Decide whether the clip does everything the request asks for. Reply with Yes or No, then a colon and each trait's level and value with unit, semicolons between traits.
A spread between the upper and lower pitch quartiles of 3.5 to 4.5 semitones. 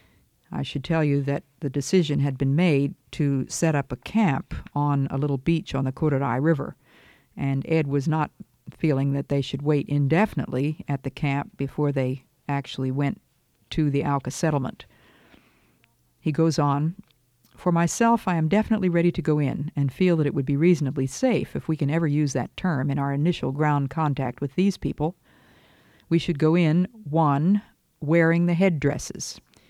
No: average, 3.0 semitones